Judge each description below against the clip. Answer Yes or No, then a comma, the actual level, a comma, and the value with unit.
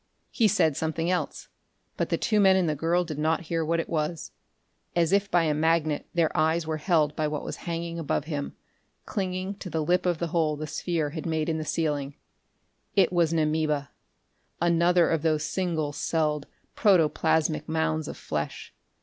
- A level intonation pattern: Yes, narrow, 1.9 semitones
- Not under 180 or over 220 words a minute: Yes, average, 185 wpm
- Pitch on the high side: No, medium, 160 Hz